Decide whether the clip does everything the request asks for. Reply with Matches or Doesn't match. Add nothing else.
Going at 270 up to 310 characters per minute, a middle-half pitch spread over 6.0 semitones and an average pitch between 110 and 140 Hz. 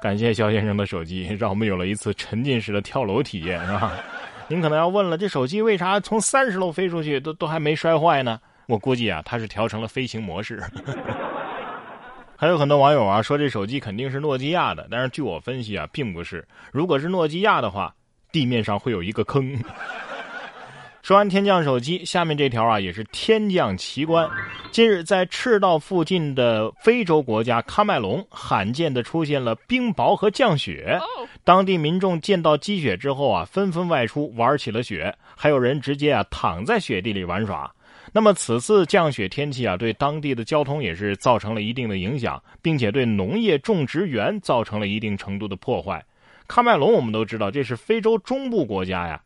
Matches